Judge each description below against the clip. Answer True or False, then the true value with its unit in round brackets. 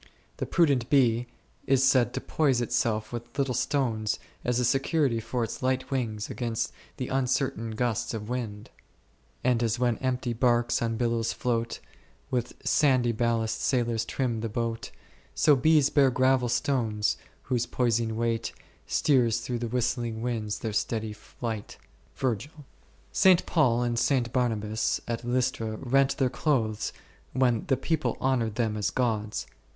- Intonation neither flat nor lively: False (2.3 semitones)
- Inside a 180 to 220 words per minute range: False (145 wpm)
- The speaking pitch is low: True (120 Hz)